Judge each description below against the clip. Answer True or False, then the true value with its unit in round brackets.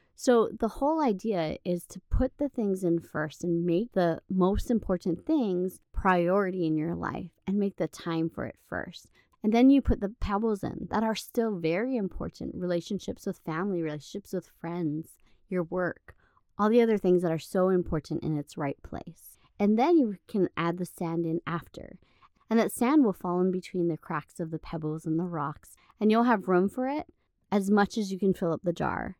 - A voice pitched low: False (185 Hz)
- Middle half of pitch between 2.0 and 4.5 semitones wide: True (4.1 semitones)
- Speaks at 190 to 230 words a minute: True (205 wpm)